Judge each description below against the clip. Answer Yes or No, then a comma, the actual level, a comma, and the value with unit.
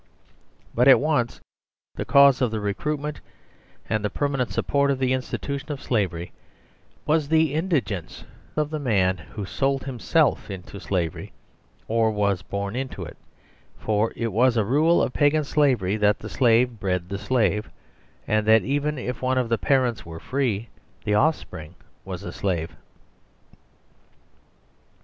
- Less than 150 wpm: Yes, average, 140 wpm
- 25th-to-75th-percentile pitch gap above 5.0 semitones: Yes, wide, 5.4 semitones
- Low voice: Yes, low, 120 Hz